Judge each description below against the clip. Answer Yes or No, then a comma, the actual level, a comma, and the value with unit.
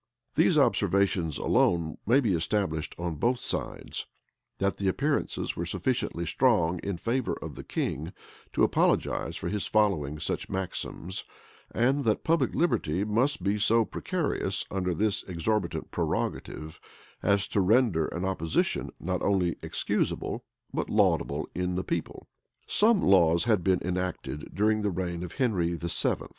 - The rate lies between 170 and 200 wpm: No, average, 145 wpm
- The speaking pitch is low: Yes, very low, 95 Hz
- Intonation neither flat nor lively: Yes, average, 4.0 semitones